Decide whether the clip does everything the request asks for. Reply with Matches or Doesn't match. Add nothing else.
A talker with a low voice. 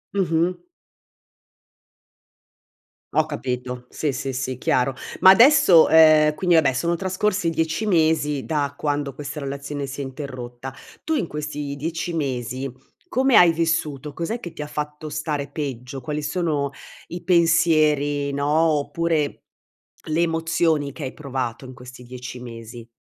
Doesn't match